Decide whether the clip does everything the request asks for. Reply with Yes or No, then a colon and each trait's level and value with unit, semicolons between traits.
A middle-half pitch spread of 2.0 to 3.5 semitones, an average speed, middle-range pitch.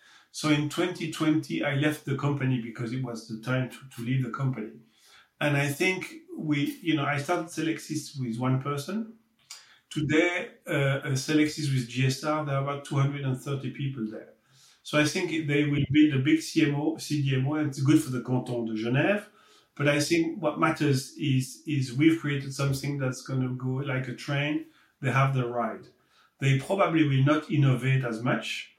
Yes: average, 2.9 semitones; average, 180 wpm; medium, 145 Hz